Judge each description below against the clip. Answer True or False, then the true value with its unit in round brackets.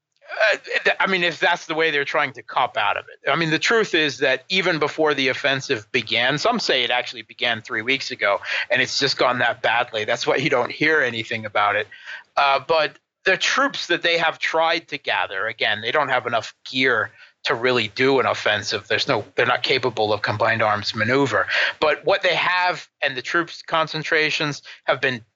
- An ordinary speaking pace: False (210 wpm)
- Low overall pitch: False (150 Hz)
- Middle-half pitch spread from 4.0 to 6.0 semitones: True (4.8 semitones)